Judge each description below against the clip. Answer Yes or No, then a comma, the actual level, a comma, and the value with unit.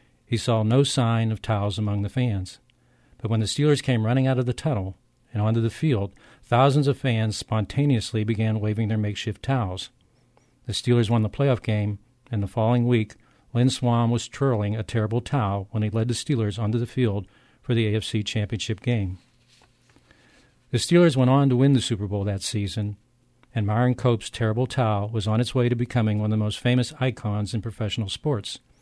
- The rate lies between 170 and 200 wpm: Yes, average, 195 wpm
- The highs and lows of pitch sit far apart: No, average, 2.7 semitones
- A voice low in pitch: Yes, low, 115 Hz